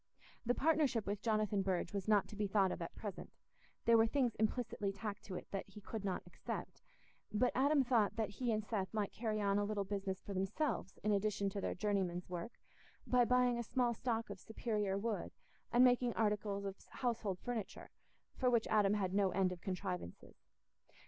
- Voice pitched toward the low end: No, high, 210 Hz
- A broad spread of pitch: No, average, 3.0 semitones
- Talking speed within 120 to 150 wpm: No, average, 190 wpm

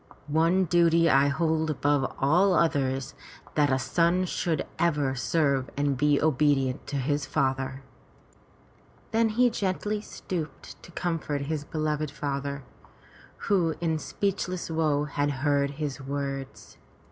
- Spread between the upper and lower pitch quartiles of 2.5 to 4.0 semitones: Yes, average, 3.2 semitones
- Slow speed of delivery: Yes, slow, 130 wpm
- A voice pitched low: No, medium, 150 Hz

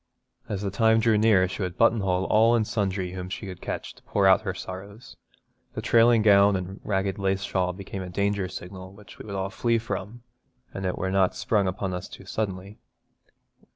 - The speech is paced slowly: No, average, 200 wpm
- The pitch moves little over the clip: Yes, narrow, 2.2 semitones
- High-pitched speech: No, low, 100 Hz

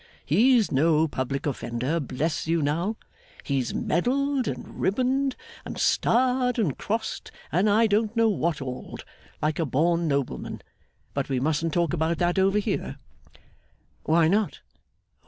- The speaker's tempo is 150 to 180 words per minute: No, average, 140 wpm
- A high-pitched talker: No, medium, 170 Hz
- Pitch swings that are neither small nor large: No, wide, 6.8 semitones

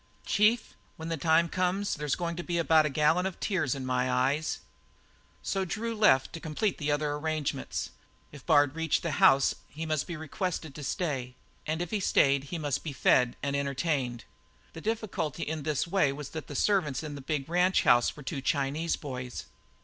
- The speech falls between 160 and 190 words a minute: No, average, 200 wpm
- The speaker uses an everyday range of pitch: Yes, average, 3.6 semitones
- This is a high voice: No, medium, 155 Hz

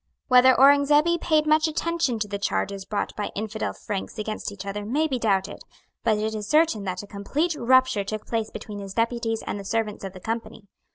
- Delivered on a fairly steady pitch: No, average, 4.7 semitones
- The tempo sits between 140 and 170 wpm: No, fast, 205 wpm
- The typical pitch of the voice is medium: No, high, 220 Hz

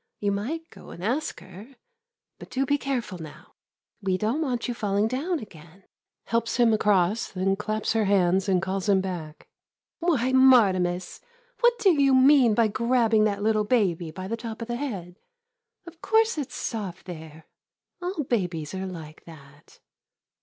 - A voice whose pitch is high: Yes, high, 215 Hz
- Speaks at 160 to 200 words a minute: Yes, average, 170 wpm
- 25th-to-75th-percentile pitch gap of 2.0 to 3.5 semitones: No, wide, 5.6 semitones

